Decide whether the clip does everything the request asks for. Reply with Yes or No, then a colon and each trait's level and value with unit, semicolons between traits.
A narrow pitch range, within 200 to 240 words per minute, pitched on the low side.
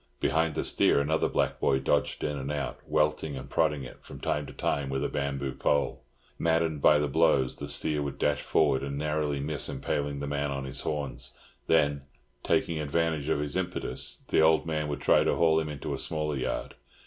Yes: narrow, 1.7 semitones; fast, 205 wpm; very low, 75 Hz